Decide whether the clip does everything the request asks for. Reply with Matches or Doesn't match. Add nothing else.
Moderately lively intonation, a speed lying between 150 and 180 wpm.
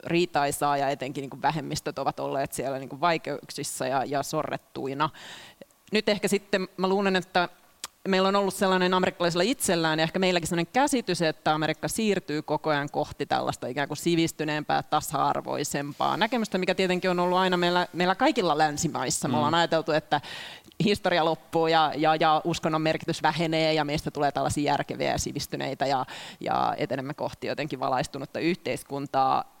Matches